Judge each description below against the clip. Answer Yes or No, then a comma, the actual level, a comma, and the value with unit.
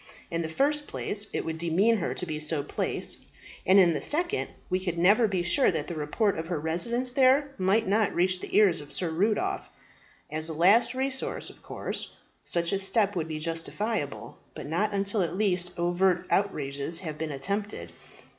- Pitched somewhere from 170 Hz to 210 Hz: Yes, medium, 185 Hz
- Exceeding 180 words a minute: Yes, average, 190 wpm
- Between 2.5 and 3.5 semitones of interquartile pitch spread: No, average, 4.7 semitones